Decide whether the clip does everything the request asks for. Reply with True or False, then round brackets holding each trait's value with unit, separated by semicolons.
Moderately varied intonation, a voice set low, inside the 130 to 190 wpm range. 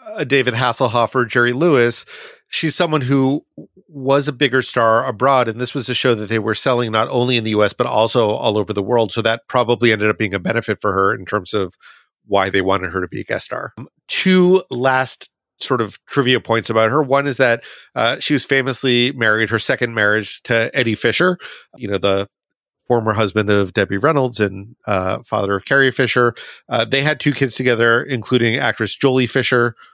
False (3.7 semitones; 120 Hz; 205 wpm)